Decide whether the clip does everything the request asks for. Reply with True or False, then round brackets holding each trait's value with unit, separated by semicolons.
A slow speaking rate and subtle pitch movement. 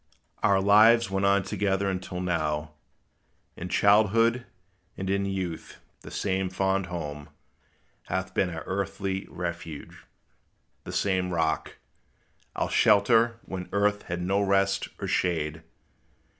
True (120 wpm; 2.1 semitones)